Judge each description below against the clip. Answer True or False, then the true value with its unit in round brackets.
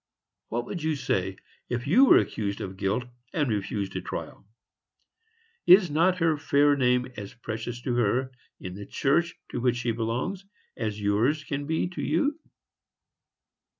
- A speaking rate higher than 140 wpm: True (155 wpm)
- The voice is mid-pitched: False (125 Hz)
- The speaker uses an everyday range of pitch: False (6.1 semitones)